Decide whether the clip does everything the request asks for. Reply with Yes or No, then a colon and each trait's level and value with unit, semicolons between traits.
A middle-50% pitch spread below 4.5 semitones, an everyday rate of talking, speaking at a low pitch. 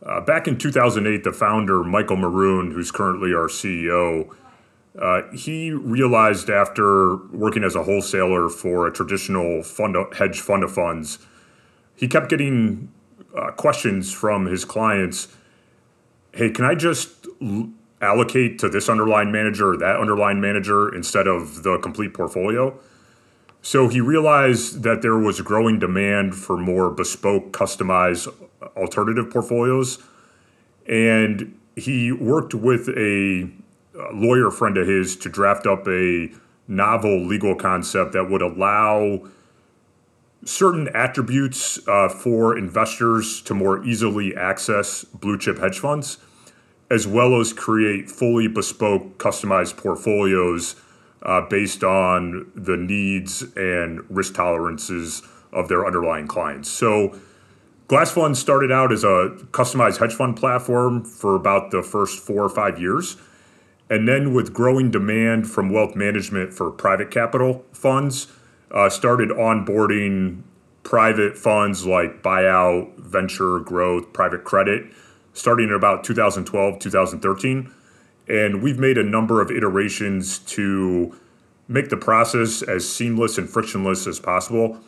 No: average, 4.0 semitones; slow, 130 wpm; low, 105 Hz